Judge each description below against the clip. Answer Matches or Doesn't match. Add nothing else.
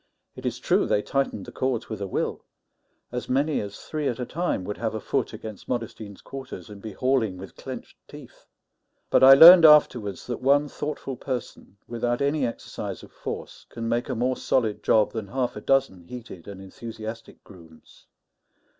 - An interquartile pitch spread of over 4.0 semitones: Matches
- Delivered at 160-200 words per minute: Matches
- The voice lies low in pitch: Matches